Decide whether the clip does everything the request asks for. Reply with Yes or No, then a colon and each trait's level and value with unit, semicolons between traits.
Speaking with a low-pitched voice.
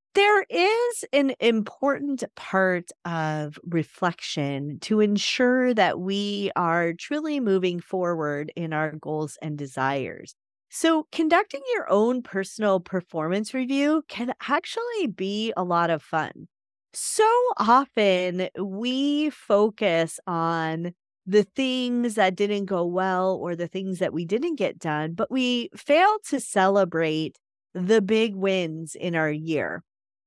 No: high, 195 Hz